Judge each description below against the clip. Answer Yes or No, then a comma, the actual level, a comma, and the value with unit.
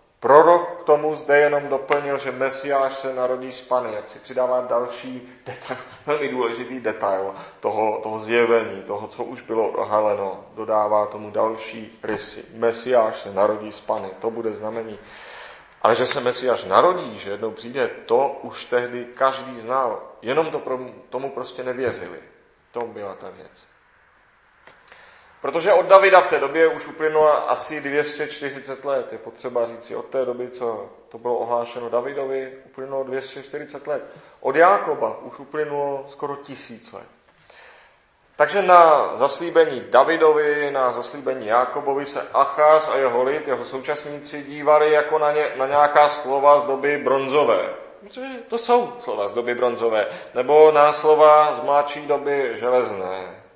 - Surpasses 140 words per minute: Yes, average, 150 wpm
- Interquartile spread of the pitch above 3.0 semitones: Yes, average, 3.6 semitones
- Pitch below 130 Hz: No, low, 135 Hz